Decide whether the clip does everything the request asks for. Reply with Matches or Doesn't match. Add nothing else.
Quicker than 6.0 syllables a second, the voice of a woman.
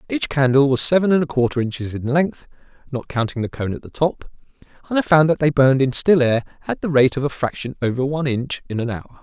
Doesn't match